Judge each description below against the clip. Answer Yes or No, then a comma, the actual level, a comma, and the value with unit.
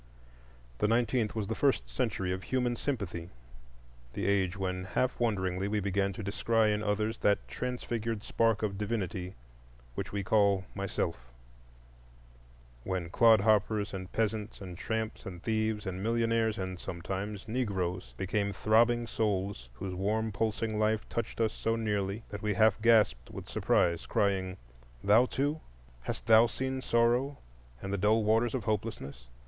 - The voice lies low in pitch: Yes, low, 105 Hz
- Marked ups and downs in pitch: No, average, 3.1 semitones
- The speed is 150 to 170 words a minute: No, average, 140 wpm